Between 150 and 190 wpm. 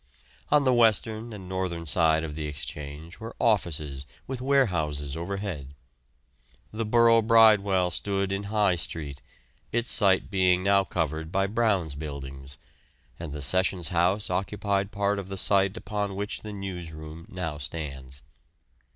No: average, 140 wpm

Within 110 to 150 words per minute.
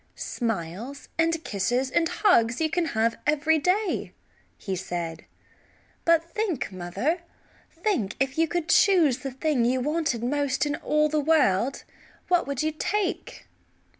Yes: average, 140 wpm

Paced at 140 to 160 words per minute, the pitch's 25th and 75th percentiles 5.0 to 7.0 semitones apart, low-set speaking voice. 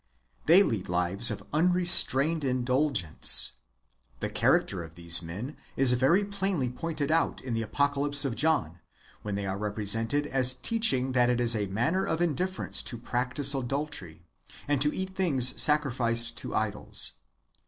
Yes: average, 150 wpm; average, 5.3 semitones; low, 130 Hz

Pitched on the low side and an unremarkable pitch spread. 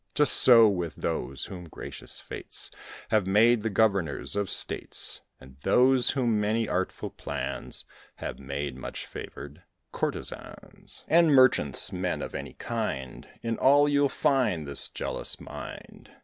No: low, 105 Hz; wide, 7.7 semitones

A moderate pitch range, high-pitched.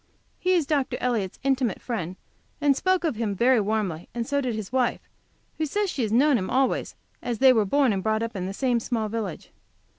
Yes: average, 4.2 semitones; high, 240 Hz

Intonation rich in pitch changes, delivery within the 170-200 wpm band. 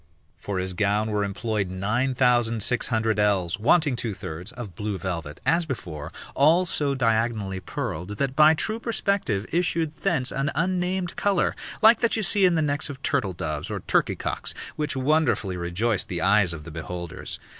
Yes: wide, 8.2 semitones; average, 175 wpm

